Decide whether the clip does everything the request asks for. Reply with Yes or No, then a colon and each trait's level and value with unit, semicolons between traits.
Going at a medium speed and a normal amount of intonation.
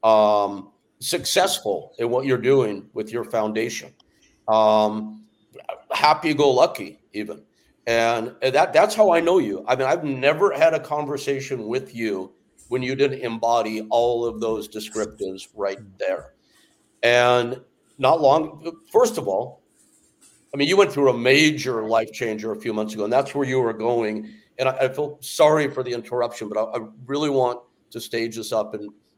Yes: average, 165 wpm; average, 4.2 semitones